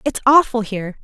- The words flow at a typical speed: Yes, average, 175 wpm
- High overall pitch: Yes, high, 235 Hz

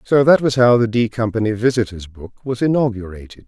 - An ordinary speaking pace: Yes, average, 190 wpm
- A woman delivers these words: No, male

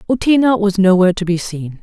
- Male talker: No, female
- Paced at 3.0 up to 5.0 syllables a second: No, 6.1 syllables/s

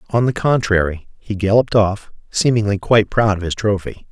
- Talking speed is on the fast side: No, average, 175 wpm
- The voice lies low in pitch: Yes, low, 105 Hz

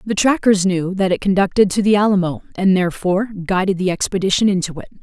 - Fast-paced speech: No, average, 190 wpm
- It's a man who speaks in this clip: No, female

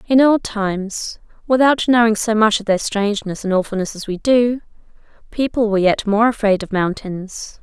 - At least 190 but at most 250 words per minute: No, average, 175 wpm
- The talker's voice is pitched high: Yes, high, 215 Hz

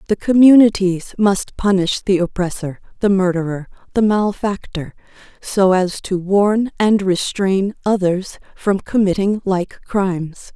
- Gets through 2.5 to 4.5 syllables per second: Yes, 4.1 syllables/s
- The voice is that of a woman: Yes, female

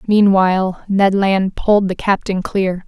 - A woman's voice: Yes, female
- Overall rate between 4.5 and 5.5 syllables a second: No, 4.1 syllables/s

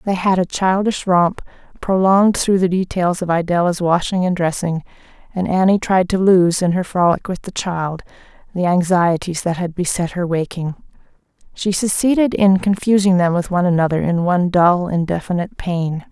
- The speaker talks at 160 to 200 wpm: Yes, average, 170 wpm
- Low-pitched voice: No, medium, 180 Hz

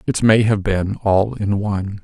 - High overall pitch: No, low, 100 Hz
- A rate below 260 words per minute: Yes, fast, 205 wpm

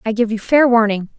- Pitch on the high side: Yes, high, 225 Hz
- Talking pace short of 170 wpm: No, fast, 255 wpm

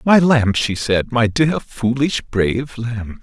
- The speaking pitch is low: Yes, low, 120 Hz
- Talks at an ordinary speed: Yes, average, 170 wpm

